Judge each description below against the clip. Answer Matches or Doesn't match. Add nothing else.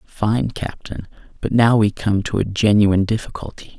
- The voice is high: Doesn't match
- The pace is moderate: Matches